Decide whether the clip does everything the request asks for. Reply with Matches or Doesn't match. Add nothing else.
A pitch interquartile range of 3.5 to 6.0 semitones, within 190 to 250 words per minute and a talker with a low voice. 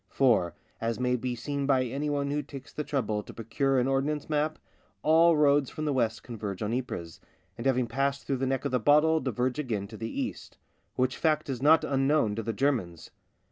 Matches